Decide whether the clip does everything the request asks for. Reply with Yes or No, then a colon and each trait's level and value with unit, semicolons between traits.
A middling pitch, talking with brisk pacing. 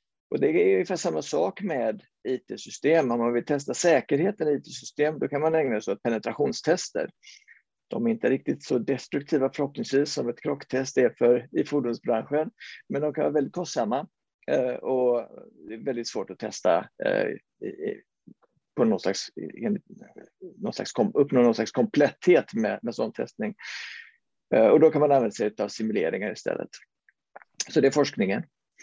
No: medium, 145 Hz; average, 155 wpm